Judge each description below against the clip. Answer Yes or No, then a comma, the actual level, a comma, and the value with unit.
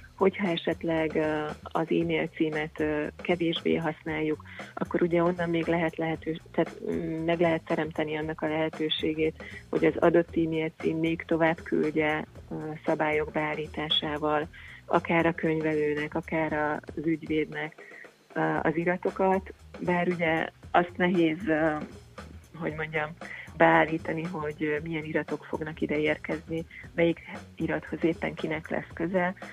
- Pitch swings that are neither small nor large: No, narrow, 1.5 semitones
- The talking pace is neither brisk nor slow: Yes, average, 115 wpm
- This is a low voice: No, medium, 160 Hz